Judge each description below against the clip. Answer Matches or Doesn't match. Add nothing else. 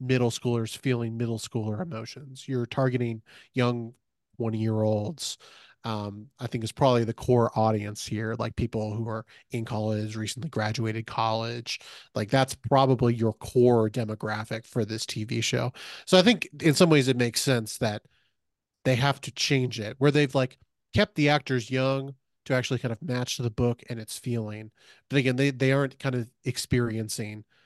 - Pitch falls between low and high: Doesn't match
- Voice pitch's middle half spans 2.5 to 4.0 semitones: Matches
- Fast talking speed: Doesn't match